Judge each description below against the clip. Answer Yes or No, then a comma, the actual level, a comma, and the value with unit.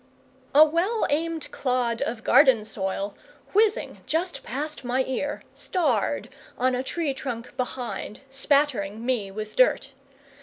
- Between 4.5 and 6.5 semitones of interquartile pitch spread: Yes, average, 5.0 semitones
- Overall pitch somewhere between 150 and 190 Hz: No, very high, 260 Hz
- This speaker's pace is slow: Yes, slow, 125 wpm